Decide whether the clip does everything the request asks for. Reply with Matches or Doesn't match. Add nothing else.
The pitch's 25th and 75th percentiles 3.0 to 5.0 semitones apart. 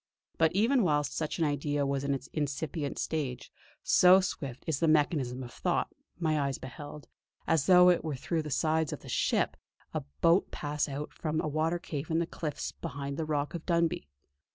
Doesn't match